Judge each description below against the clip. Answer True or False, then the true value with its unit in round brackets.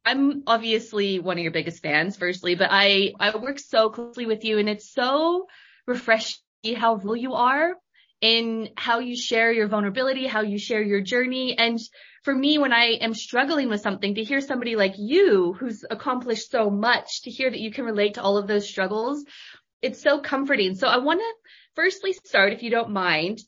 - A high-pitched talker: True (230 Hz)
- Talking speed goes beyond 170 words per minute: True (195 wpm)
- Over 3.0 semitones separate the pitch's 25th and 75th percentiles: True (4.1 semitones)